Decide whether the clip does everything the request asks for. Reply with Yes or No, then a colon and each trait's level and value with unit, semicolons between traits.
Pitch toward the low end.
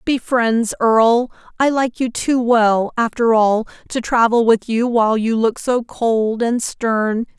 No: high, 230 Hz